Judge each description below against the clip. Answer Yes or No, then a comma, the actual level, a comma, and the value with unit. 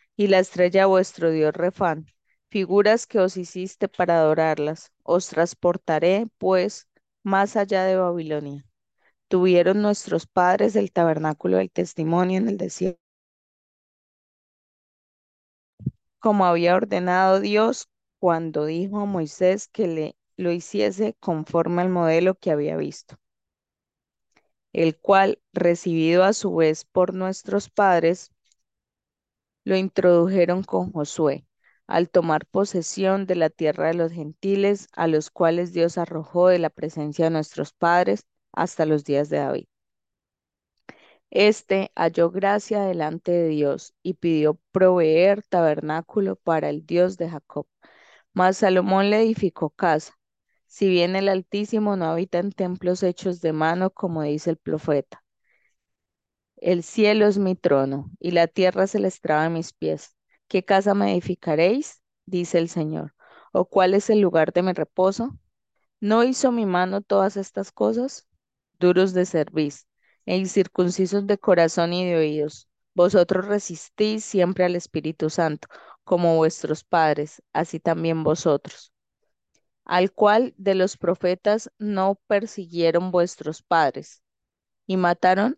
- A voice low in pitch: No, medium, 180 Hz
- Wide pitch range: No, average, 3.2 semitones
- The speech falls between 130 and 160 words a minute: Yes, average, 135 wpm